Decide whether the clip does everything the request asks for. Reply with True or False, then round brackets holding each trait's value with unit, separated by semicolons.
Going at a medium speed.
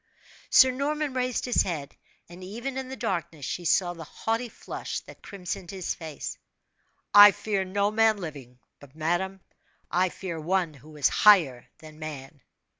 True (160 wpm)